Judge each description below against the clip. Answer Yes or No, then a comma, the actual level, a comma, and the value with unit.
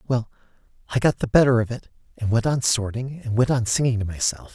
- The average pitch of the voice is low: Yes, low, 120 Hz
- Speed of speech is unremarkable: No, fast, 225 wpm